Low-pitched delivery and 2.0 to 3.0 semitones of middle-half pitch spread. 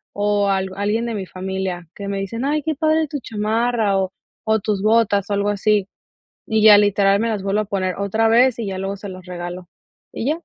No: high, 205 Hz; average, 2.7 semitones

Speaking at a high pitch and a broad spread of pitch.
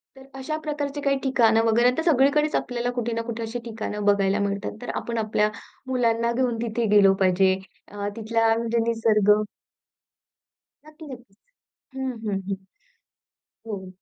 No: high, 230 Hz; average, 3.3 semitones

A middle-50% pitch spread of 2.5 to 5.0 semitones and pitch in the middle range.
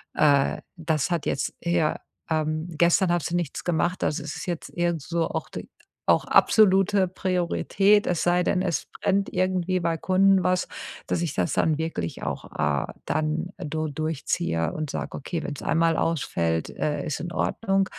Yes: average, 2.9 semitones; medium, 170 Hz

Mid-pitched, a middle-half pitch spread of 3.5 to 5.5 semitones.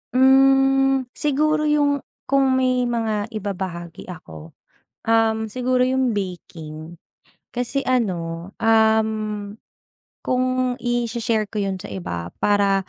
No: high, 225 Hz; average, 5.0 semitones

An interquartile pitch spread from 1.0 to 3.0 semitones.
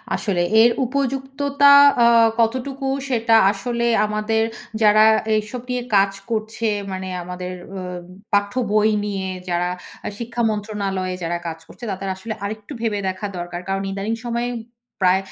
No: average, 3.5 semitones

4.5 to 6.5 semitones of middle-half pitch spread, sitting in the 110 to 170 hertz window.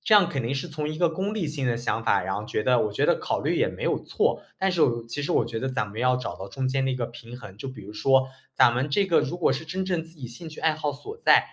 Yes: average, 5.3 semitones; low, 135 Hz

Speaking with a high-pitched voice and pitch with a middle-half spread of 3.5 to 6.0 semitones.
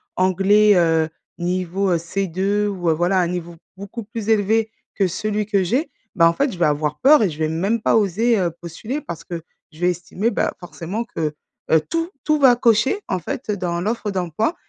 Yes: high, 195 Hz; average, 4.3 semitones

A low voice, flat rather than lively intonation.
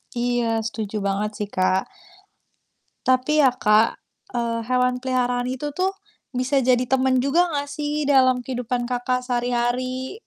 No: very high, 250 Hz; narrow, 1.6 semitones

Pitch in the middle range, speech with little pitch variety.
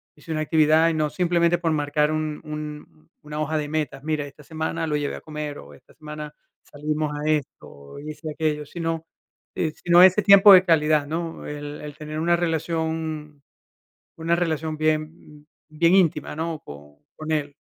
Yes: medium, 155 Hz; narrow, 1.5 semitones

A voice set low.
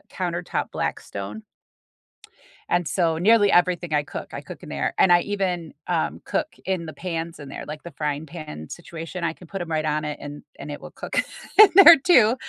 No: medium, 170 Hz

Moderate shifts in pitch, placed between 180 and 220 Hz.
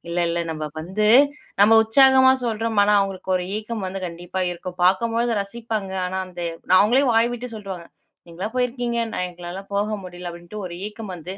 Yes: average, 4.1 semitones; high, 200 Hz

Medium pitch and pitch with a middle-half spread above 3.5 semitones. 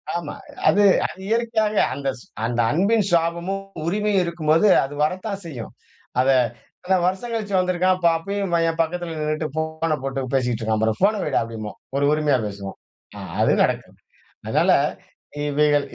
Yes: medium, 165 Hz; wide, 5.5 semitones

